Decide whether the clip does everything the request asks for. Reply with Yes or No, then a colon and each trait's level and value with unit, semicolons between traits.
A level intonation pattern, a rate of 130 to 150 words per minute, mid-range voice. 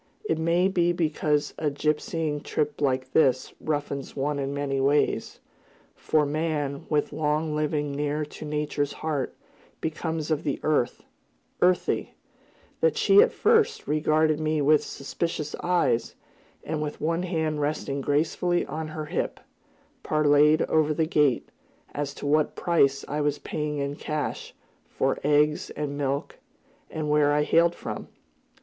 Yes: narrow, 1.6 semitones; average, 145 wpm; medium, 150 Hz